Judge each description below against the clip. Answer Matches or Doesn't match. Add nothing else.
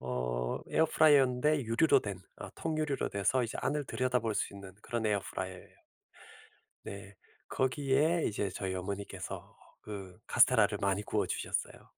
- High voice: Doesn't match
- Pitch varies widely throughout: Matches